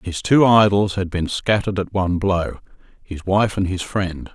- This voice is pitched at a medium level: No, very low, 95 Hz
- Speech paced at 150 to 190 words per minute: Yes, average, 180 wpm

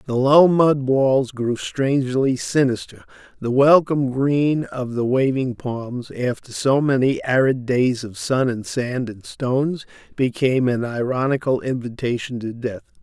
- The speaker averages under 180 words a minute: Yes, average, 145 wpm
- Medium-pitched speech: No, low, 130 Hz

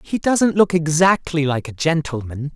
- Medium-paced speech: Yes, average, 165 wpm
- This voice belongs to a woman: No, male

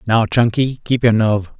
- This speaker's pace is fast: No, average, 190 wpm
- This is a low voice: Yes, low, 115 Hz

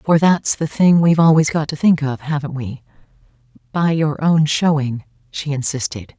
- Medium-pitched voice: Yes, medium, 150 Hz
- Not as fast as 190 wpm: Yes, average, 155 wpm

